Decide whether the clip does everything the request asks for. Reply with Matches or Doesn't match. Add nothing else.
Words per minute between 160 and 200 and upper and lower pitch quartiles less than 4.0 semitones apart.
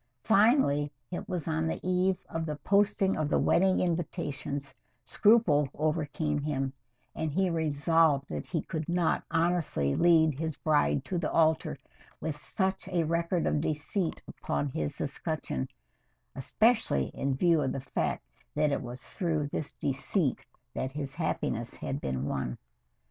Doesn't match